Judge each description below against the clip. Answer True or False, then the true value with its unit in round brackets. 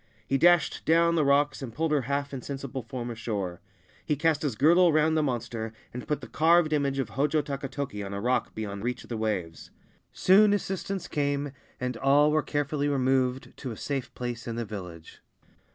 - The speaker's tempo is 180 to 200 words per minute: True (190 wpm)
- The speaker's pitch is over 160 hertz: False (135 Hz)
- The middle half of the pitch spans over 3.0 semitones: True (4.2 semitones)